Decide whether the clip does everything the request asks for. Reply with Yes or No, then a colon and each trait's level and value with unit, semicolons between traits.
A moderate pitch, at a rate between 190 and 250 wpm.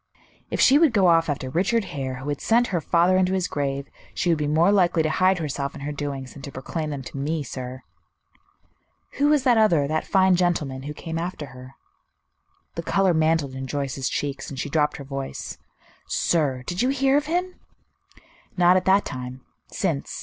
Yes: medium, 155 Hz; average, 200 wpm